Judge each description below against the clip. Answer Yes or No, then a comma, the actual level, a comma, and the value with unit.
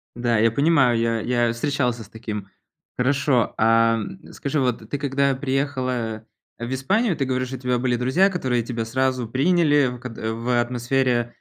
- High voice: No, low, 125 Hz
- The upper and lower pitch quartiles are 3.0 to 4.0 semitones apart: No, narrow, 2.6 semitones